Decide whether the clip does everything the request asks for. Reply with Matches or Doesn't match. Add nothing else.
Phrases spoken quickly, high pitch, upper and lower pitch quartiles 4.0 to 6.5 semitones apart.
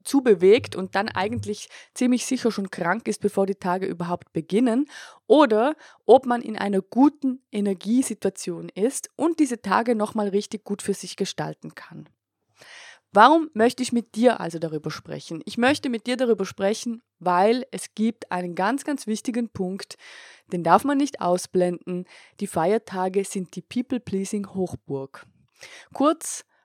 Doesn't match